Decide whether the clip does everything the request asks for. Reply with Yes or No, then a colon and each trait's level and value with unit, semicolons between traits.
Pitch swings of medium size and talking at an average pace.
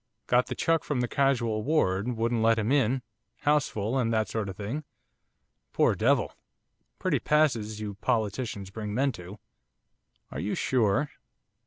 Yes: average, 4.0 semitones; average, 155 wpm